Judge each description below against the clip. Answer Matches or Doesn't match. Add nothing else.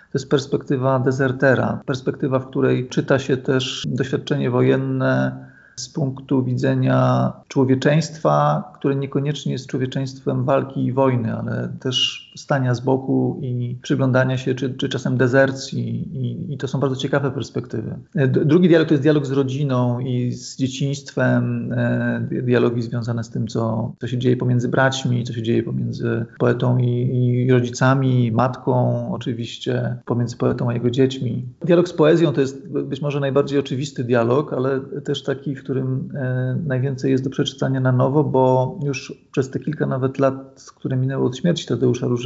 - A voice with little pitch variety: Matches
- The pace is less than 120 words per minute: Doesn't match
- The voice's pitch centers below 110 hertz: Doesn't match